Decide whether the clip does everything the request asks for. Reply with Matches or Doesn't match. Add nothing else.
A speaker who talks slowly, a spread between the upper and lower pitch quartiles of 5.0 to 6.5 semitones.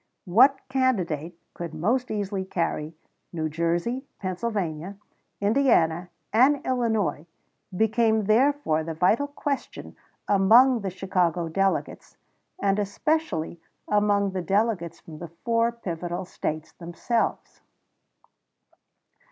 Matches